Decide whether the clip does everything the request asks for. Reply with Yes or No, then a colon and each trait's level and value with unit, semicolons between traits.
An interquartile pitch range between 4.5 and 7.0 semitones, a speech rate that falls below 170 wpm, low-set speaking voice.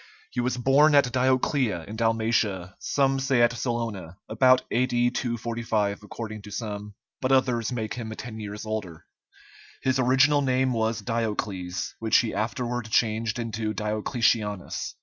No: average, 2.9 semitones; average, 140 wpm; low, 115 Hz